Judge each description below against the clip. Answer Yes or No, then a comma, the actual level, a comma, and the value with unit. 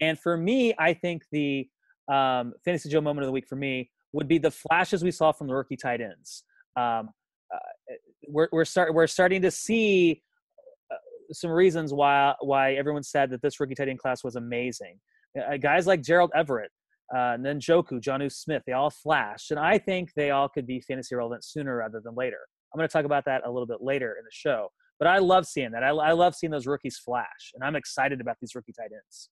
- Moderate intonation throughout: Yes, average, 4.8 semitones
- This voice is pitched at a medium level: Yes, medium, 145 Hz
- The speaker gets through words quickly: Yes, fast, 220 wpm